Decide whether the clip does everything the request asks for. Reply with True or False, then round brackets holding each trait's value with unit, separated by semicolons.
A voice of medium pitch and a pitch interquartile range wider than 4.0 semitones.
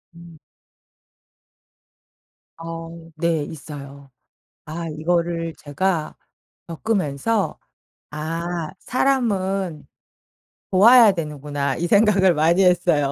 False (170 Hz; 3.7 semitones)